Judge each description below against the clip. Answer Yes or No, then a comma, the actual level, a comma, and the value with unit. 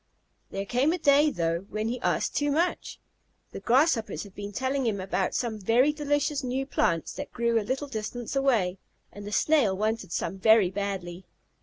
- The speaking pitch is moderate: No, high, 230 Hz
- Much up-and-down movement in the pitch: Yes, wide, 5.7 semitones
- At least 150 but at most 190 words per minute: Yes, average, 180 wpm